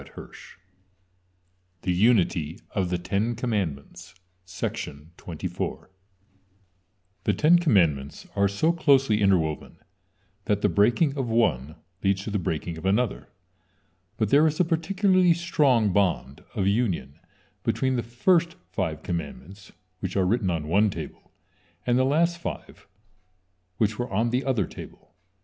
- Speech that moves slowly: Yes, slow, 125 wpm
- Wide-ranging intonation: Yes, wide, 5.8 semitones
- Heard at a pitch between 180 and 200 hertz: No, low, 100 Hz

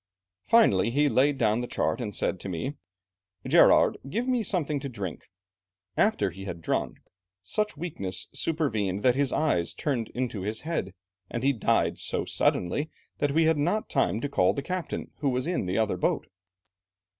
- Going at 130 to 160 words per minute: No, average, 175 wpm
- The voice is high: No, low, 130 Hz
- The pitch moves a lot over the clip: Yes, wide, 8.0 semitones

